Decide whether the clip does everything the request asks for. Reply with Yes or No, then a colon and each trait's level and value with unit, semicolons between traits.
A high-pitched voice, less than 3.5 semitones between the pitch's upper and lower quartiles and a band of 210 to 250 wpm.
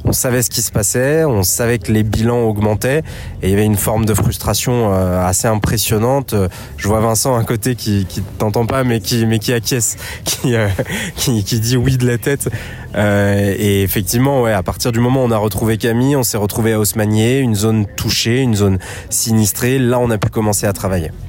No: low, 110 Hz; average, 2.8 semitones; average, 215 wpm